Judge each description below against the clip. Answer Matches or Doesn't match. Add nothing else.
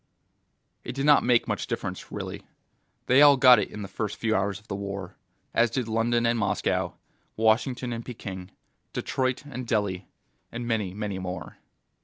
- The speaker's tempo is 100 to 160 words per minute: Doesn't match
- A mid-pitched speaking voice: Doesn't match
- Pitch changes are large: Doesn't match